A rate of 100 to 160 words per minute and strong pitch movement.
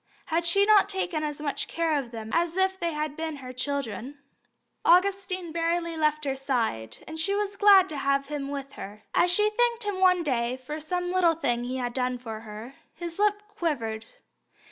No: average, 195 wpm; wide, 5.8 semitones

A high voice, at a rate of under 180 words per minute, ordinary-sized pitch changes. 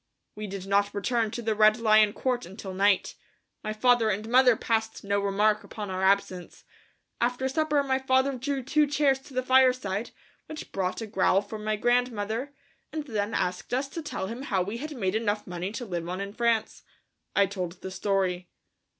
No: high, 215 Hz; average, 190 wpm; average, 4.2 semitones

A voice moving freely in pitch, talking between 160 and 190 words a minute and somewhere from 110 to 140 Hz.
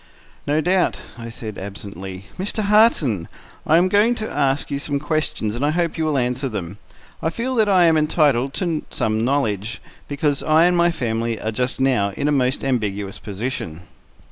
Yes: wide, 6.7 semitones; average, 185 wpm; low, 135 Hz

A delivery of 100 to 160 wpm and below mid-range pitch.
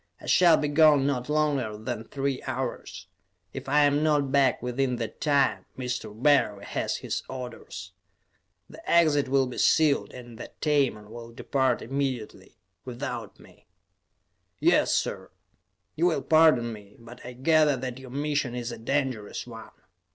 Yes: average, 150 wpm; low, 130 Hz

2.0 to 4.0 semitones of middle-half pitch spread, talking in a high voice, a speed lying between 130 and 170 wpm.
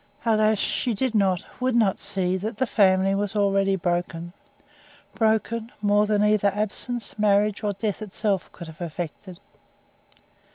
Yes: narrow, 2.4 semitones; high, 205 Hz; average, 140 wpm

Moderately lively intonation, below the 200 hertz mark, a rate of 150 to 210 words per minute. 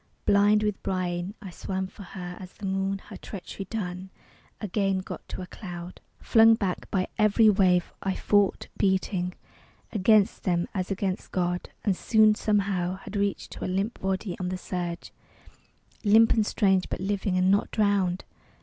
No: narrow, 2.0 semitones; high, 190 Hz; average, 165 wpm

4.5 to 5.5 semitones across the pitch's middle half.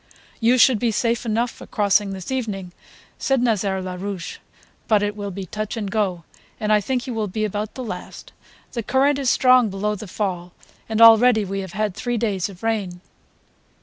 No: average, 3.0 semitones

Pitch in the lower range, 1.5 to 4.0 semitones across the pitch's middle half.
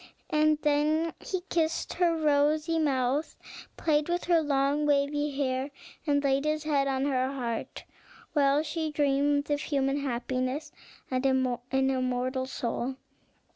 No: very high, 285 Hz; narrow, 2.4 semitones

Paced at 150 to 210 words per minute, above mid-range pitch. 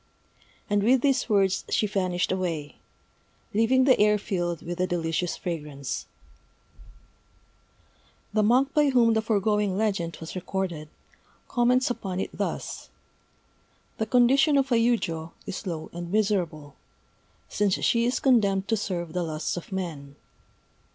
No: slow, 135 wpm; high, 195 Hz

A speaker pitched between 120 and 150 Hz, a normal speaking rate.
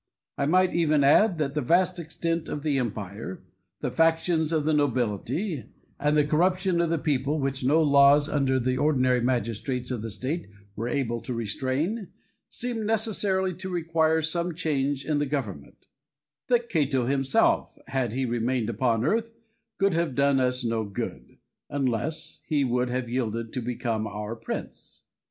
Yes: medium, 140 Hz; average, 160 wpm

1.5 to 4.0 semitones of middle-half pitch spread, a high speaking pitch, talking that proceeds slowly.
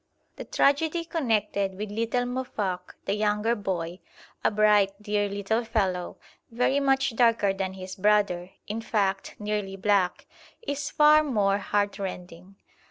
Yes: average, 3.2 semitones; high, 210 Hz; slow, 130 wpm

